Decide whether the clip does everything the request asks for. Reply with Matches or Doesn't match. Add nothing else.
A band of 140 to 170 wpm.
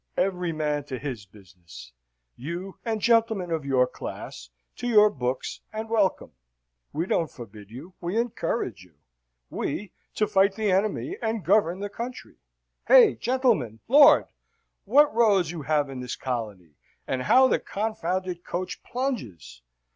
Matches